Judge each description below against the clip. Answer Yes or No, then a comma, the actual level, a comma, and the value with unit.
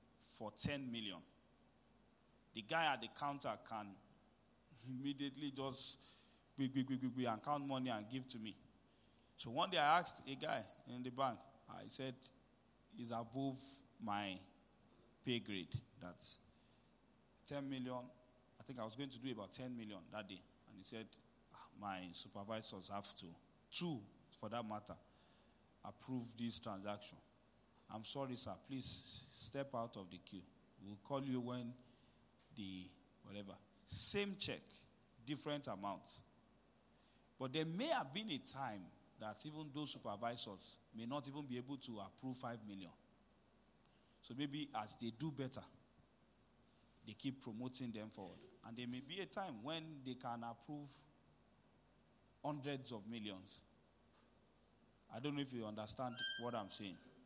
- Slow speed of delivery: No, average, 145 wpm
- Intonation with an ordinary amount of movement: Yes, average, 4.0 semitones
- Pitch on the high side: No, low, 125 Hz